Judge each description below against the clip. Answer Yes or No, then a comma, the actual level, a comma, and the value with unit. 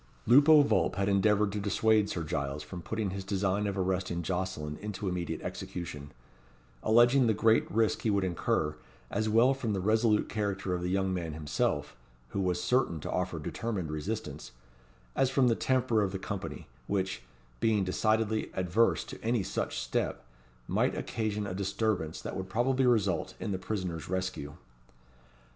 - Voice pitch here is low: Yes, low, 100 Hz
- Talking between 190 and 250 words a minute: No, average, 165 wpm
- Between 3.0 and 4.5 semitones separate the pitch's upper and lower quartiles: Yes, average, 3.5 semitones